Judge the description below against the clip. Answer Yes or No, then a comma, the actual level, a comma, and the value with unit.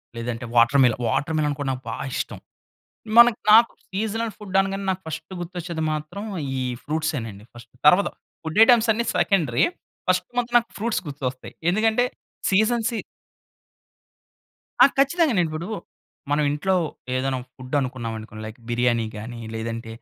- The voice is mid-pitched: Yes, medium, 160 Hz